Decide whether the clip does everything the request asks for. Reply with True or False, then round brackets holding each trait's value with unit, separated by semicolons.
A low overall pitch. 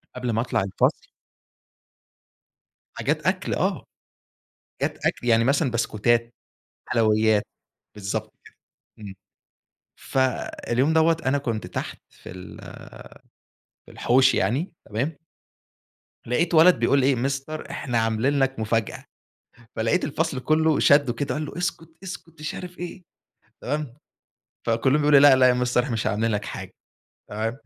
True (130 Hz)